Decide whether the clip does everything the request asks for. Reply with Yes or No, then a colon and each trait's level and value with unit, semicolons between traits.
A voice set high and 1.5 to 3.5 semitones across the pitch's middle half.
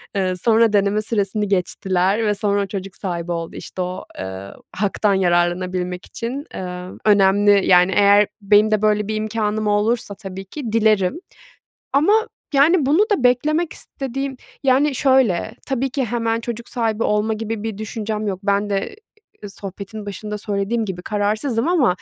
Yes: high, 210 Hz; average, 2.9 semitones